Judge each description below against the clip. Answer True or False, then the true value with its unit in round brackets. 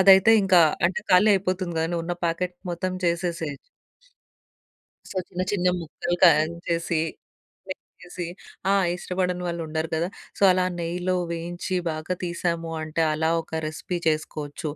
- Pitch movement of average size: False (2.0 semitones)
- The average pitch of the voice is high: False (170 Hz)